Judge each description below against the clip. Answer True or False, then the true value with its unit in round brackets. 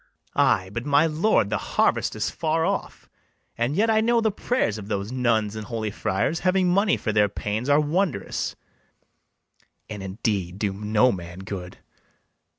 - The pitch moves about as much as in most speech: False (8.2 semitones)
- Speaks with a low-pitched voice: True (110 Hz)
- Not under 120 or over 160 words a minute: False (170 wpm)